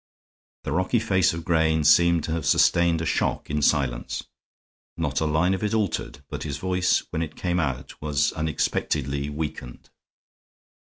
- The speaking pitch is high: No, very low, 80 Hz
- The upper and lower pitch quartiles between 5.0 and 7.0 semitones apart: No, average, 2.9 semitones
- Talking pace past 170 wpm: No, average, 155 wpm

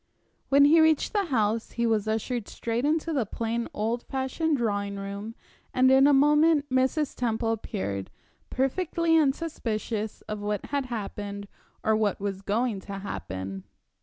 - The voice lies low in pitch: No, high, 230 Hz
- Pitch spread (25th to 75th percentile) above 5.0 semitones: Yes, wide, 5.4 semitones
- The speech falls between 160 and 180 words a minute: No, average, 150 wpm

